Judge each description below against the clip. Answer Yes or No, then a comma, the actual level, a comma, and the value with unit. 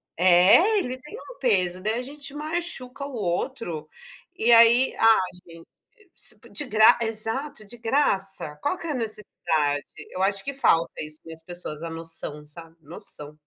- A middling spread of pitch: No, wide, 8.1 semitones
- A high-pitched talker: Yes, high, 215 Hz